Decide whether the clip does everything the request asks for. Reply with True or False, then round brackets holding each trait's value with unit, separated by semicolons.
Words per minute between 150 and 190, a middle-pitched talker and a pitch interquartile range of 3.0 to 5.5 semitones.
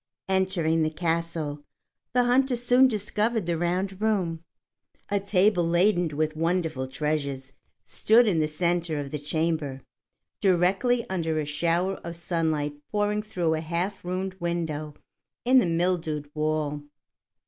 False (135 wpm; 170 Hz; 3.7 semitones)